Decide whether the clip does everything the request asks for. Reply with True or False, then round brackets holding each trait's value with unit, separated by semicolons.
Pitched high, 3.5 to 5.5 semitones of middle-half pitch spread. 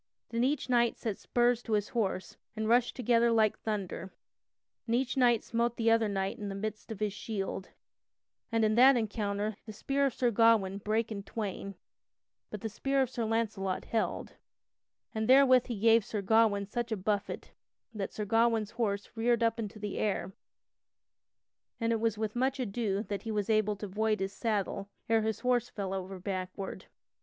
False (220 Hz; 2.5 semitones)